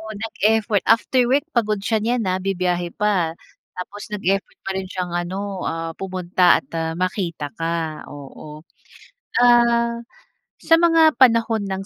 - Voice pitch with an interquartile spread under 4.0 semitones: No, average, 4.6 semitones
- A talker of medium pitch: No, high, 195 Hz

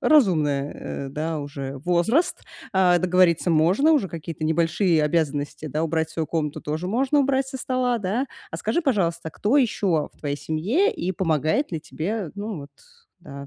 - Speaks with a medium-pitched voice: Yes, medium, 170 Hz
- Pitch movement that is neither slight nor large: No, wide, 5.8 semitones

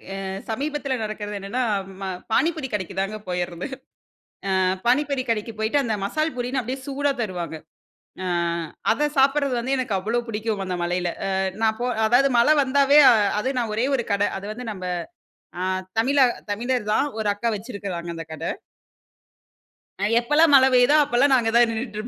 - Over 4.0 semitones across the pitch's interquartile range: Yes, average, 4.6 semitones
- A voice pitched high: Yes, high, 235 Hz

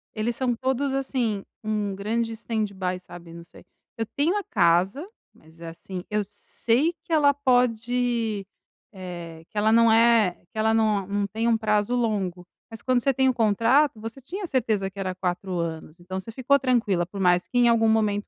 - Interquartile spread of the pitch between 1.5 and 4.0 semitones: No, average, 4.4 semitones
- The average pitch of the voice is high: Yes, high, 220 Hz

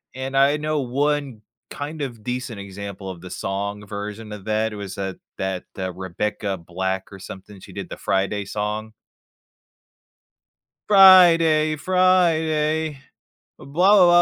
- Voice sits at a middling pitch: No, low, 110 Hz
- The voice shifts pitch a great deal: Yes, wide, 7.6 semitones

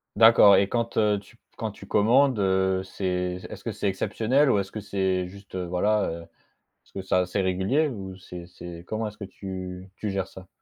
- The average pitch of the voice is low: Yes, very low, 95 Hz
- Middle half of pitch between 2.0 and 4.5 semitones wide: Yes, narrow, 2.5 semitones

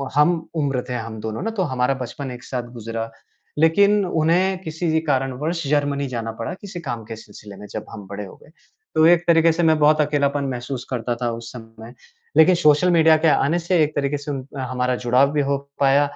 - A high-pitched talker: No, medium, 140 Hz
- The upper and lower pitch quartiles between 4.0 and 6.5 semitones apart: Yes, average, 4.8 semitones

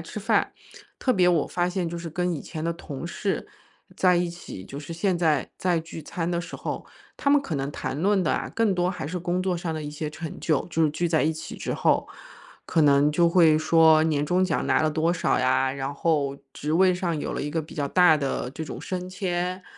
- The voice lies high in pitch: No, medium, 165 Hz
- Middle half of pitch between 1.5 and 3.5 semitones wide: Yes, average, 2.9 semitones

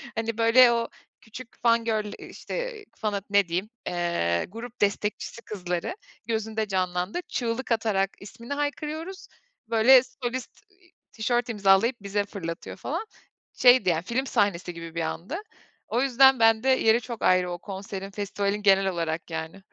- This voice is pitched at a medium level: No, high, 220 Hz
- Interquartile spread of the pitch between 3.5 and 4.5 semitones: Yes, average, 4.1 semitones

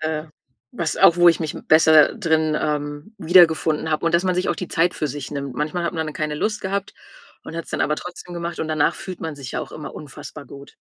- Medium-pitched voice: Yes, medium, 160 Hz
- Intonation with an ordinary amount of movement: No, narrow, 2.3 semitones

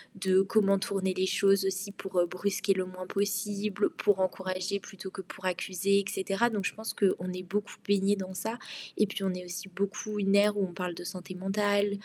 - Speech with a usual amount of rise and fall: No, narrow, 1.5 semitones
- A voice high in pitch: Yes, high, 195 Hz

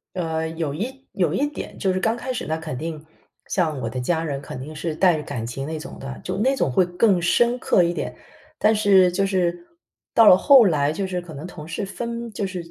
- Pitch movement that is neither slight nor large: Yes, average, 4.4 semitones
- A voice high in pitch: No, medium, 175 Hz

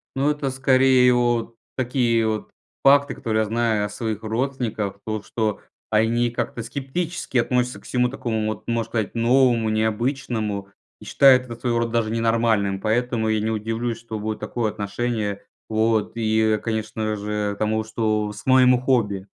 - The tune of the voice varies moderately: No, narrow, 2.3 semitones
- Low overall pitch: Yes, low, 115 Hz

